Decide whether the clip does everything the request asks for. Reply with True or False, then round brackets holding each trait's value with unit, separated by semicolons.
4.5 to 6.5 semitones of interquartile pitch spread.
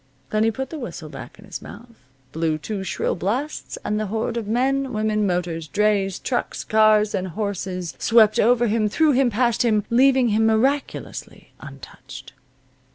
False (3.1 semitones)